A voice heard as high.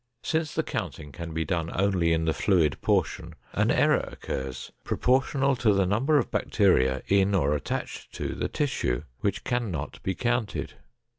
No: very low, 95 Hz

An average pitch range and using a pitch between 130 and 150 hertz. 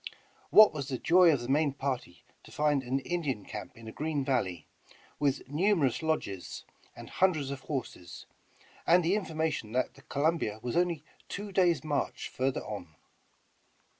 Yes: average, 4.4 semitones; medium, 140 Hz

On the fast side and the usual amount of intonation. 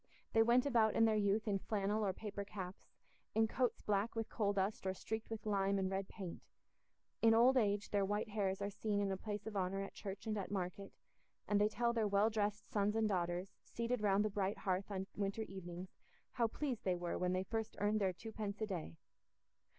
No: fast, 215 wpm; narrow, 2.1 semitones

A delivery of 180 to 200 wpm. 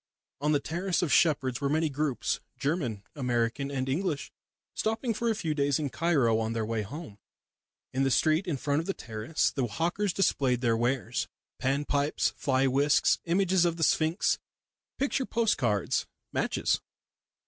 No: average, 160 wpm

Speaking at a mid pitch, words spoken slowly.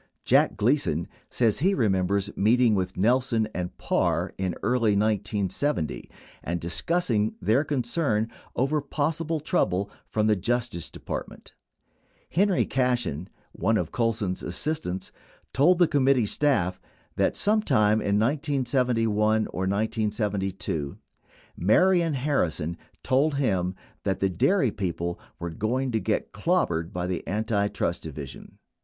No: low, 110 Hz; slow, 120 wpm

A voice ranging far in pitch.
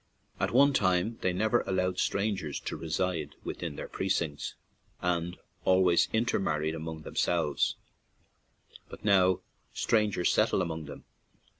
No: average, 3.4 semitones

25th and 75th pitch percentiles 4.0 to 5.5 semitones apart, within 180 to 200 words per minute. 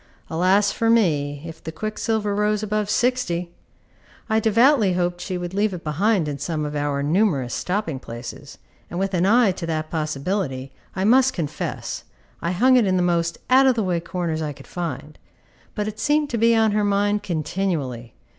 Yes: average, 5.2 semitones; average, 185 wpm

